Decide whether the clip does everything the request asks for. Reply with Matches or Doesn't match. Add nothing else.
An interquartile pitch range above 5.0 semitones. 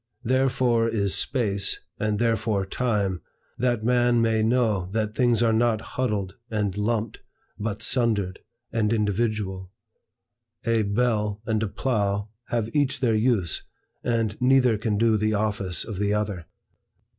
Doesn't match